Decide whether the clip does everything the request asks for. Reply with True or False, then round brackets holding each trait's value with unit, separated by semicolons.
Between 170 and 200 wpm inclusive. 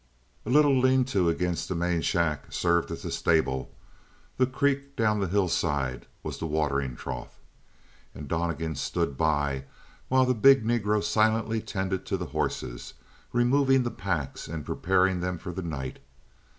False (155 wpm)